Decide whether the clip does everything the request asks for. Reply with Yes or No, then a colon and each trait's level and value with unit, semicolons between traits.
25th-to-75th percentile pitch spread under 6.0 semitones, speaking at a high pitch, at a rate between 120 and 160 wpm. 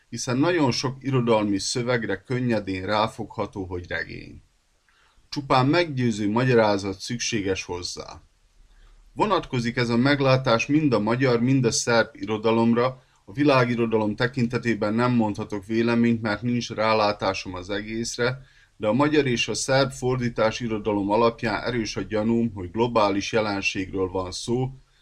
No: average, 2.9 semitones; low, 115 Hz; average, 125 wpm